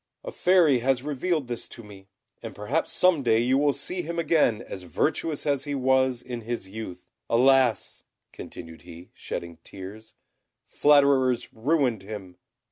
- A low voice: Yes, low, 125 Hz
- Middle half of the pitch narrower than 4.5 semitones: No, average, 5.3 semitones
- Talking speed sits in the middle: Yes, average, 150 wpm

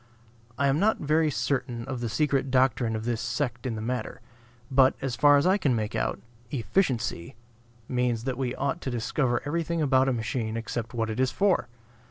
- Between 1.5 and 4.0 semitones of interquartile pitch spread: Yes, average, 3.4 semitones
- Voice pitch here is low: Yes, low, 130 Hz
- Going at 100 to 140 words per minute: No, average, 195 wpm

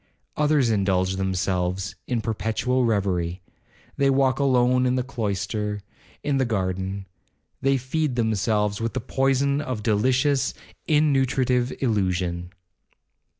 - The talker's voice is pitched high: No, low, 115 Hz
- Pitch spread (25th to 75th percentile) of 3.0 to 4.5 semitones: No, average, 5.2 semitones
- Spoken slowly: Yes, slow, 110 wpm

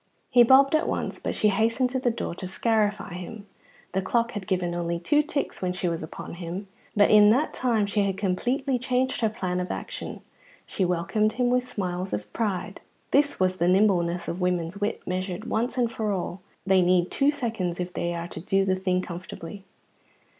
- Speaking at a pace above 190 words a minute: Yes, average, 200 wpm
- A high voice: Yes, high, 195 Hz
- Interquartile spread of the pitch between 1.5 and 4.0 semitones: No, average, 4.4 semitones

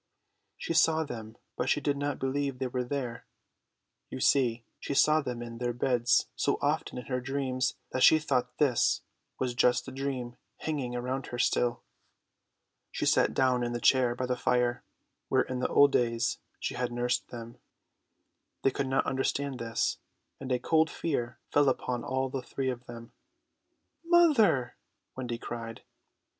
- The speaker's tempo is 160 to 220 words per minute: Yes, average, 165 wpm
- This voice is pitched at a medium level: No, low, 125 Hz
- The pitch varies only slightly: Yes, narrow, 2.1 semitones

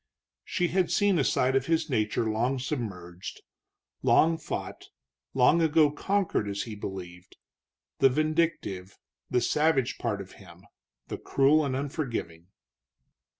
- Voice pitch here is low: Yes, low, 130 Hz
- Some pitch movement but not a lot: No, wide, 7.4 semitones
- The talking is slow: Yes, slow, 130 wpm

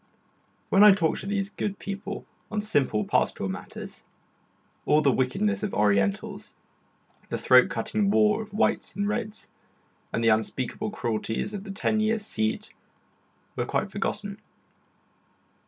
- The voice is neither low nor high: No, high, 195 Hz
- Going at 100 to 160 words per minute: Yes, average, 140 wpm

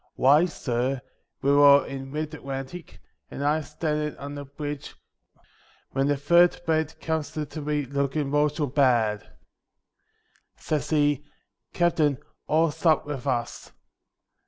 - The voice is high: No, medium, 145 Hz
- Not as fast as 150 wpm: Yes, slow, 135 wpm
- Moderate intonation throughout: No, narrow, 2.1 semitones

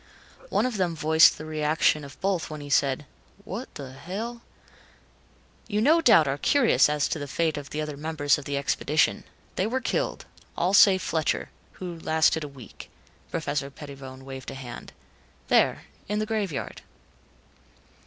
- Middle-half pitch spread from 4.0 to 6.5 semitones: Yes, average, 5.1 semitones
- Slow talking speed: No, average, 165 wpm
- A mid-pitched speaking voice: Yes, medium, 155 Hz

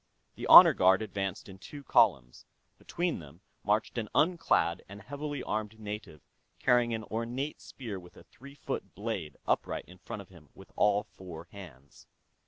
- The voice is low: Yes, low, 105 Hz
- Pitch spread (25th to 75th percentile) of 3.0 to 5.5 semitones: Yes, average, 4.6 semitones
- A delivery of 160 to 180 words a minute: Yes, average, 165 wpm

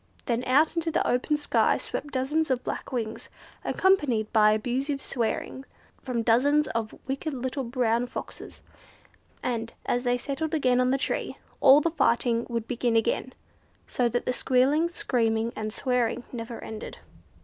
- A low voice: No, very high, 250 Hz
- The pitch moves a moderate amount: Yes, average, 3.1 semitones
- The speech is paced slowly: No, average, 155 wpm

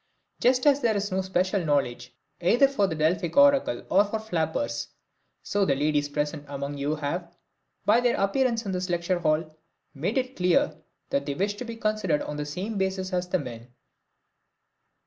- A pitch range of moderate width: No, wide, 5.9 semitones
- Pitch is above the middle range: No, medium, 180 Hz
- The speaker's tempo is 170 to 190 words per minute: Yes, average, 180 wpm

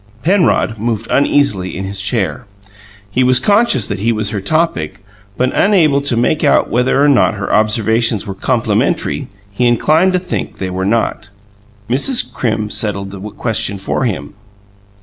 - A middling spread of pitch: No, wide, 5.8 semitones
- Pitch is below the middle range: Yes, low, 115 Hz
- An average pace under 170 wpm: Yes, average, 160 wpm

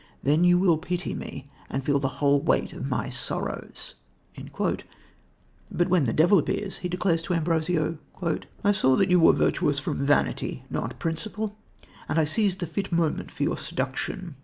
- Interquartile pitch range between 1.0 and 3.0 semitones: No, average, 3.8 semitones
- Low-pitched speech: No, medium, 165 Hz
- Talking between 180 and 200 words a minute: No, average, 170 wpm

